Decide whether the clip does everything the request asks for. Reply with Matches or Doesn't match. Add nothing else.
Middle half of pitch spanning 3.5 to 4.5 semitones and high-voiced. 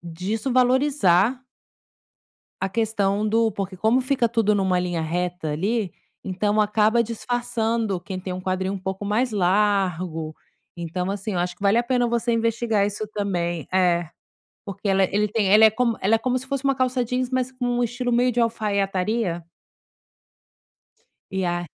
Matches